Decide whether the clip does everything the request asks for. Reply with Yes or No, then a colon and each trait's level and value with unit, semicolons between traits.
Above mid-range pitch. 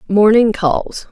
Yes: high, 210 Hz